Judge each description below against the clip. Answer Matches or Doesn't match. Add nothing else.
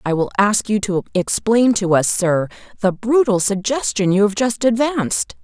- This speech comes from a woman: Matches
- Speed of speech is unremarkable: Matches